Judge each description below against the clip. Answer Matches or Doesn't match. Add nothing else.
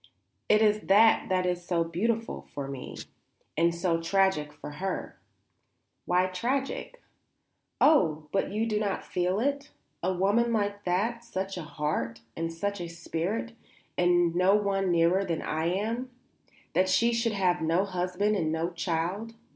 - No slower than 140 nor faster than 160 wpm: Matches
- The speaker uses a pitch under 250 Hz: Matches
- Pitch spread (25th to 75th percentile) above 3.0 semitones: Matches